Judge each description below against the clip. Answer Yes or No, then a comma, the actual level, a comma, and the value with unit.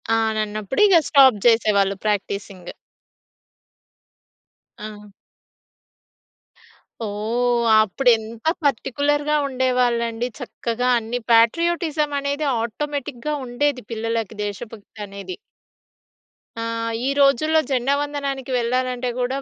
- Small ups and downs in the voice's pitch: No, average, 3.9 semitones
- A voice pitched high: Yes, high, 245 Hz